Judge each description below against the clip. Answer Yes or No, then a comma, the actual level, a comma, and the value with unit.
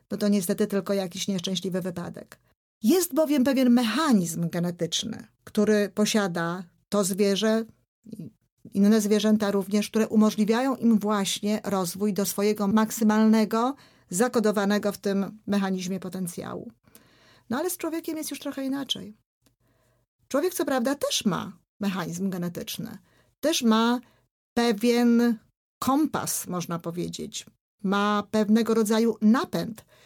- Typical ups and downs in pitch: Yes, average, 3.2 semitones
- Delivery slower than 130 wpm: Yes, average, 115 wpm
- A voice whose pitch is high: Yes, high, 210 Hz